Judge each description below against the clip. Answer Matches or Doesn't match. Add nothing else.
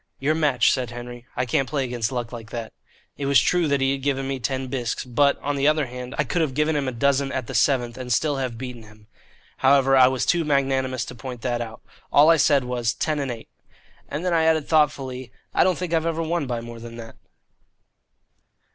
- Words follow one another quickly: Matches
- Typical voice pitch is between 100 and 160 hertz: Matches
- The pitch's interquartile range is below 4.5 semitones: Matches